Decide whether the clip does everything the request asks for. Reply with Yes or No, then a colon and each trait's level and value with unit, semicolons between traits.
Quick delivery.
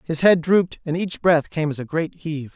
Yes: fast, 260 wpm